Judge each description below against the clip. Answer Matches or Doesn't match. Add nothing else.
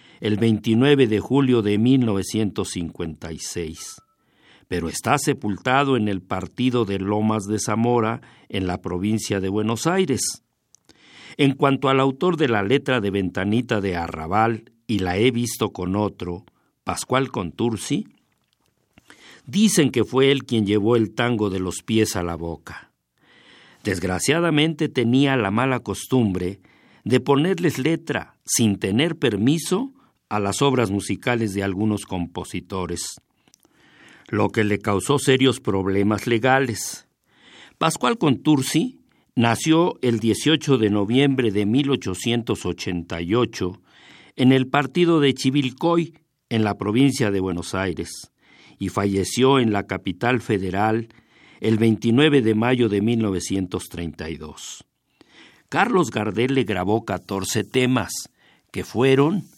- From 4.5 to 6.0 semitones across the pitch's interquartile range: Matches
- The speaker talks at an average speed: Doesn't match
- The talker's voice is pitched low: Matches